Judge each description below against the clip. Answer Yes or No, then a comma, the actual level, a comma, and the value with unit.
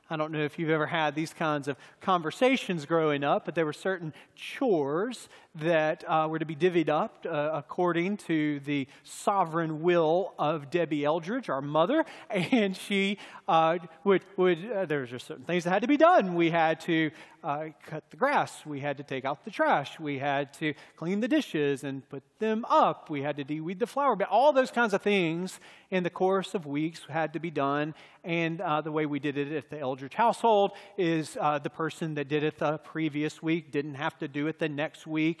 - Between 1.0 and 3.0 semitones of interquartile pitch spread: No, average, 3.6 semitones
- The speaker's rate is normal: No, fast, 215 wpm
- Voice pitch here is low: No, medium, 160 Hz